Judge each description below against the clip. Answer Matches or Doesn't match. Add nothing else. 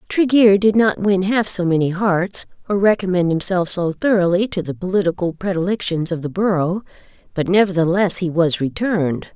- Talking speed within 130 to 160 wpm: Matches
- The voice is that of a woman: Matches